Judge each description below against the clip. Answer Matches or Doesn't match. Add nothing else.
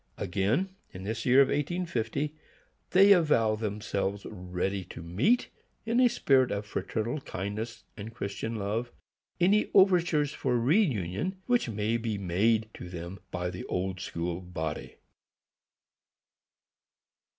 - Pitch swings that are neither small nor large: Doesn't match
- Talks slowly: Matches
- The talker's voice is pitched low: Matches